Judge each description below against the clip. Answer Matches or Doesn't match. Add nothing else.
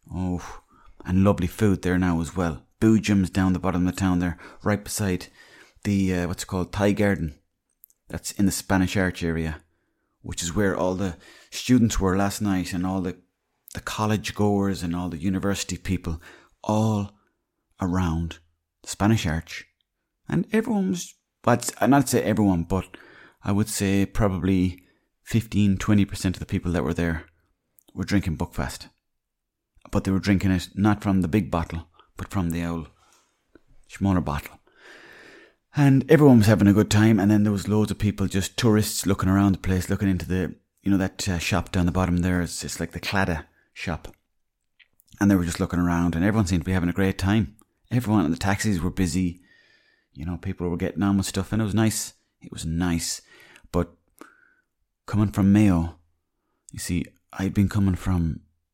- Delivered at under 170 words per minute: Doesn't match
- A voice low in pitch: Matches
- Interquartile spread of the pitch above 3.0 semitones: Doesn't match